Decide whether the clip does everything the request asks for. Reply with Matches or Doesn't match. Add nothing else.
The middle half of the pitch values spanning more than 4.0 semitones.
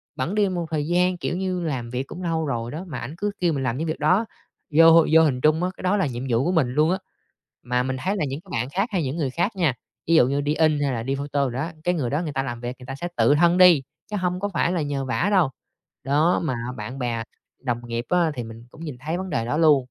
Matches